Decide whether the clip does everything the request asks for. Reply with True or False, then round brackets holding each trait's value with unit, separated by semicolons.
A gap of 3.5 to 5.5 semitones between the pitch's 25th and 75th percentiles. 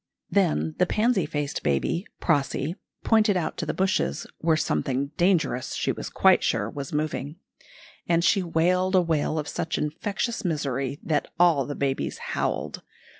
True (4.4 semitones)